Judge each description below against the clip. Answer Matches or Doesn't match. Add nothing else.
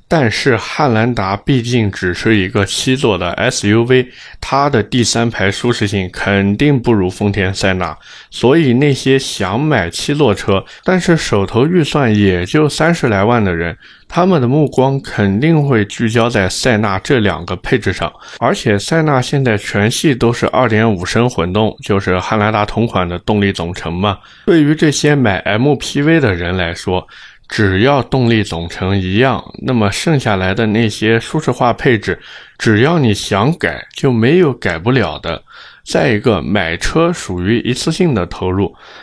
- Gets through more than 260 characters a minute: Doesn't match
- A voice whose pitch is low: Matches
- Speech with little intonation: Doesn't match